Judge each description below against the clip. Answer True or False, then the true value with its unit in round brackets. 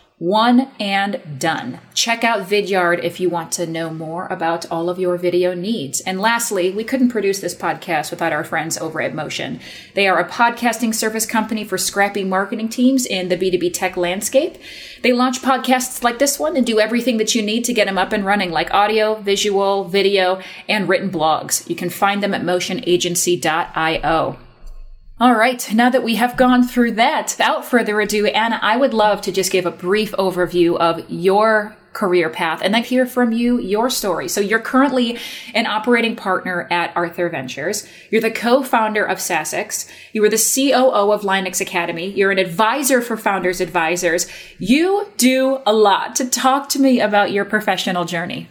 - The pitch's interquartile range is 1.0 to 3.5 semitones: False (4.6 semitones)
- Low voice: False (205 Hz)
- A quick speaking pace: False (185 wpm)